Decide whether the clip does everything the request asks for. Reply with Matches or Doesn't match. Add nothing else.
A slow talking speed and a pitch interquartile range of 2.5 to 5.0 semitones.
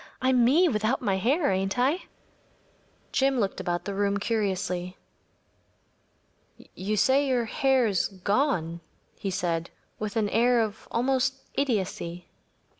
Doesn't match